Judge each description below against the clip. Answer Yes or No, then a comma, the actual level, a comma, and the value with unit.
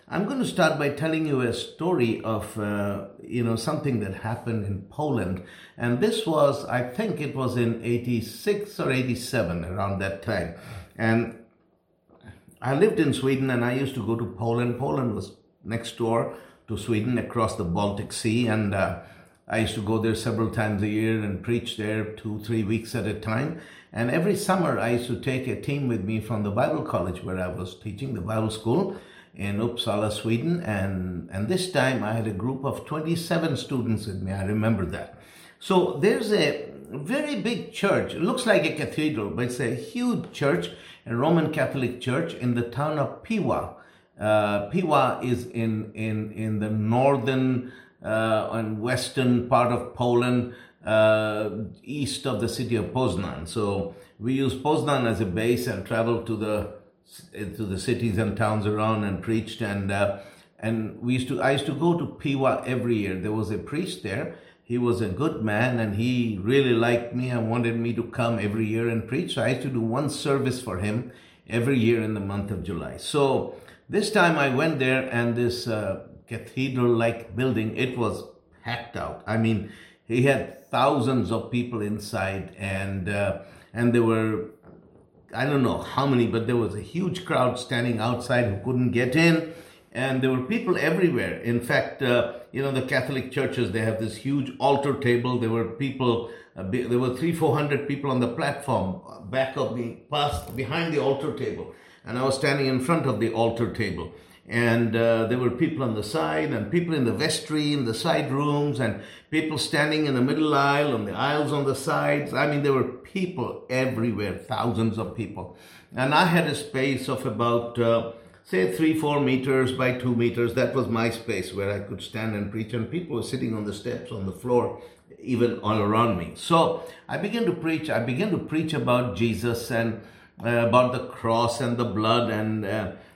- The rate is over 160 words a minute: Yes, average, 195 wpm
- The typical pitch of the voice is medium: No, low, 120 Hz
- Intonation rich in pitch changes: No, average, 3.6 semitones